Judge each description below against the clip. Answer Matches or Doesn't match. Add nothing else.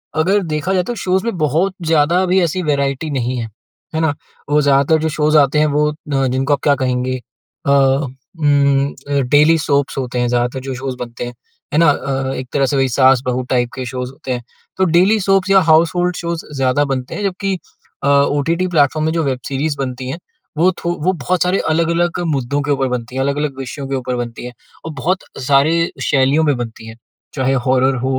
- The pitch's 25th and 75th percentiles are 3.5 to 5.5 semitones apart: Matches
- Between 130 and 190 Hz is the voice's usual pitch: Matches